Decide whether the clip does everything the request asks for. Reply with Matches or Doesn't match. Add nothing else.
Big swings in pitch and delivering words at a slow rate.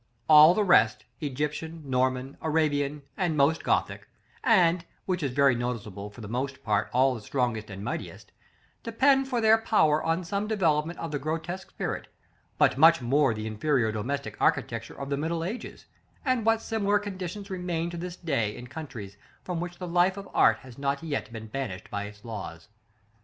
Doesn't match